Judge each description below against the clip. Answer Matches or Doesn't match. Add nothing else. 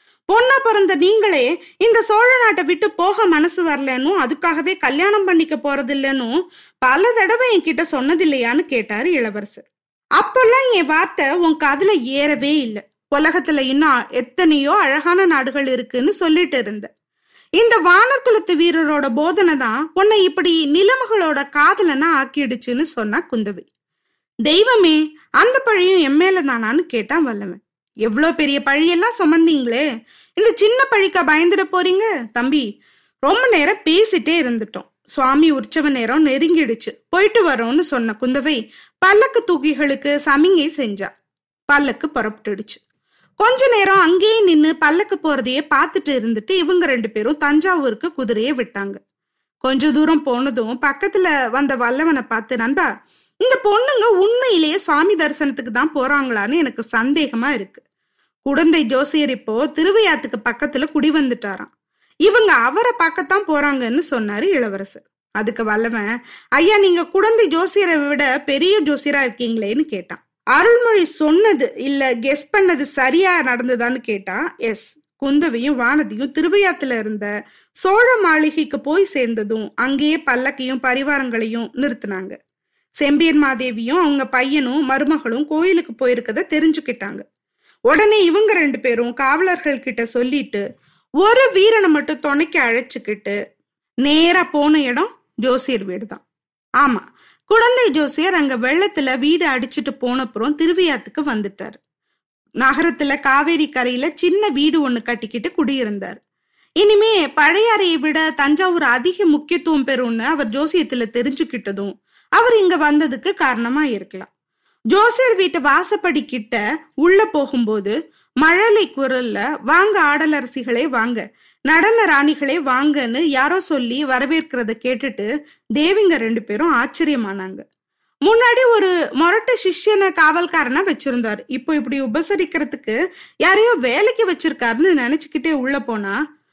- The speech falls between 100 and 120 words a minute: Matches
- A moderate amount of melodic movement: Doesn't match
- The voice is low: Doesn't match